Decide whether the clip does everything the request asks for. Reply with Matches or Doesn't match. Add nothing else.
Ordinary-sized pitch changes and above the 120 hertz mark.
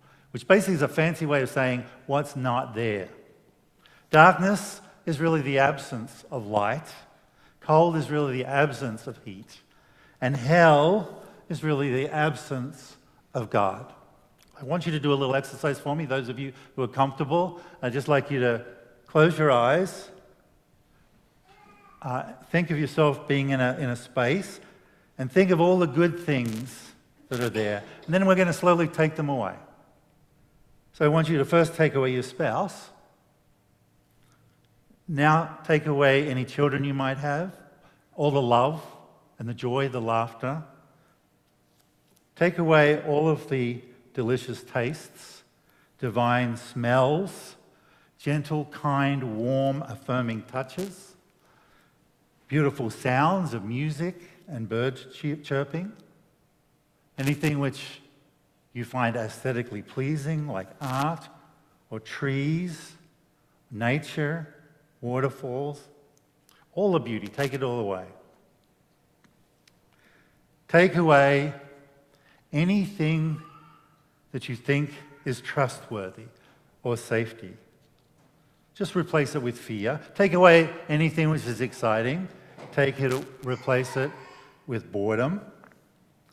Matches